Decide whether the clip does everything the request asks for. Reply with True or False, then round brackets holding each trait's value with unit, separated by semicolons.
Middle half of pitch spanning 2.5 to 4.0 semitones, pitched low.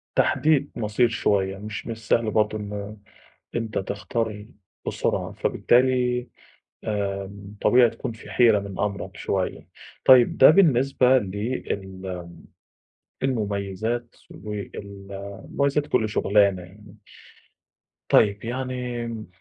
True (3.5 semitones; 110 Hz)